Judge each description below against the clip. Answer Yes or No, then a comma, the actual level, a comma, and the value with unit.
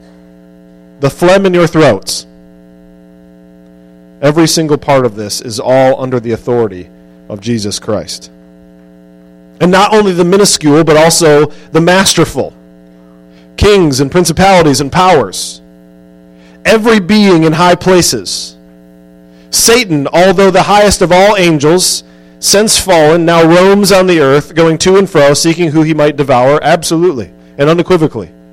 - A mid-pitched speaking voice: Yes, medium, 145 Hz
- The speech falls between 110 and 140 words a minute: Yes, slow, 135 wpm